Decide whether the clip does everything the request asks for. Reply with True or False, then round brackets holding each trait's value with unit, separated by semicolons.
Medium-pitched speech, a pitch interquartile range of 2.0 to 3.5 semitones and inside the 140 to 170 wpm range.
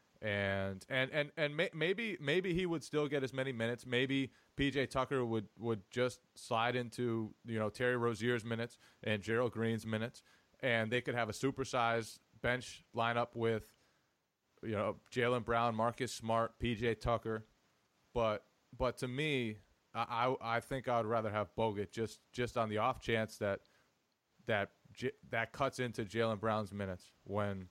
False (115 Hz; 2.6 semitones; 165 wpm)